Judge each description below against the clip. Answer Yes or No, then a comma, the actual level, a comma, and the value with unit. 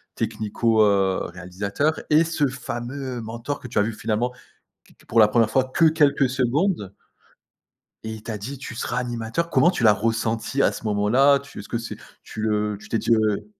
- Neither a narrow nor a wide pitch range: Yes, average, 4.2 semitones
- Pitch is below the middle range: Yes, low, 115 Hz